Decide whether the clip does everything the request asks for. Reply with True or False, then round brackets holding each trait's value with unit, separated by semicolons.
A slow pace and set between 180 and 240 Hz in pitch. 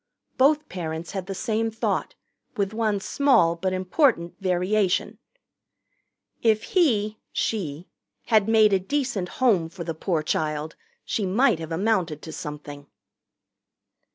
True (125 wpm; 190 Hz)